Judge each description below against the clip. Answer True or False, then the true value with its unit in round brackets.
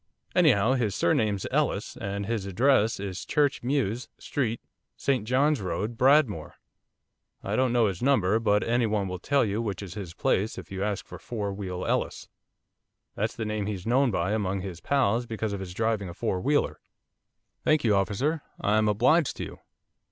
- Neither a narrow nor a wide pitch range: True (4.0 semitones)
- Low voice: True (105 Hz)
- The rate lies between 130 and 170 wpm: False (180 wpm)